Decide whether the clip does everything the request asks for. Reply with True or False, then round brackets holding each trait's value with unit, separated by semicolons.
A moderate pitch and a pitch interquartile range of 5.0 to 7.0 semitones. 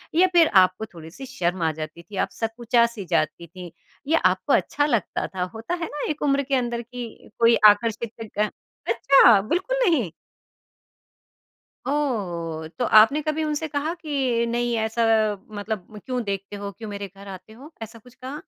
False (230 Hz; 5.6 semitones)